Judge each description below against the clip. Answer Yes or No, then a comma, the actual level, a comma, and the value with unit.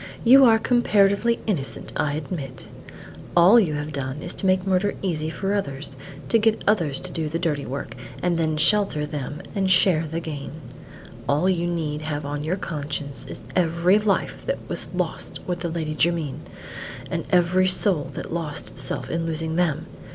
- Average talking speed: Yes, average, 175 wpm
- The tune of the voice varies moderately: Yes, average, 4.0 semitones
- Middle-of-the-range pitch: Yes, medium, 165 Hz